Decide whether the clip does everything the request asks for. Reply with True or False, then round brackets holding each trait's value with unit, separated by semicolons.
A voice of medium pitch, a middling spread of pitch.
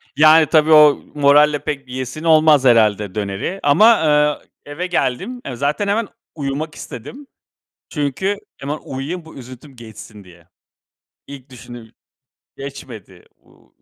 True (145 Hz; 4.0 semitones)